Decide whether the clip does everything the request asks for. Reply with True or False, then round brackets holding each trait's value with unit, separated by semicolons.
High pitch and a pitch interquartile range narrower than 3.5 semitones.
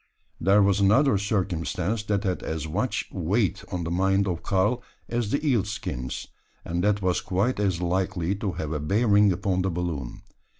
False (95 Hz; 2.9 semitones)